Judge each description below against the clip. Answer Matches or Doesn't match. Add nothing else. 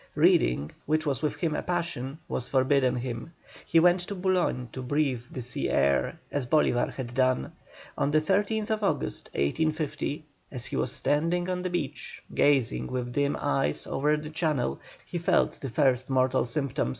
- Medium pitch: Matches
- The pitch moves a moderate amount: Matches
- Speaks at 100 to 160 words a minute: Doesn't match